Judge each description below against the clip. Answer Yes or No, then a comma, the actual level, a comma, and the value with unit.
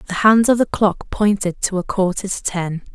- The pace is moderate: No, fast, 225 wpm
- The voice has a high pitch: Yes, high, 195 Hz